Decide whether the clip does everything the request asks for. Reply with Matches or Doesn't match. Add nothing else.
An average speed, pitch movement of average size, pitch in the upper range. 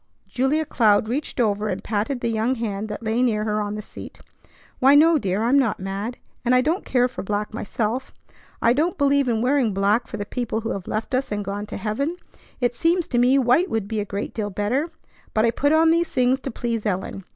Doesn't match